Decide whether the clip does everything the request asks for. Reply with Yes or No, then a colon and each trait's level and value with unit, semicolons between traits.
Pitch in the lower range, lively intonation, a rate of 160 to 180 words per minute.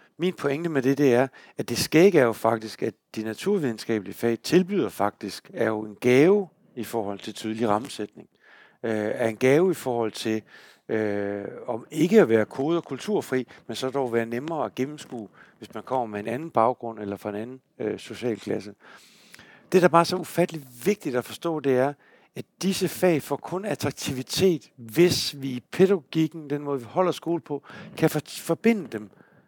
No: low, 130 Hz; wide, 6.6 semitones; average, 195 wpm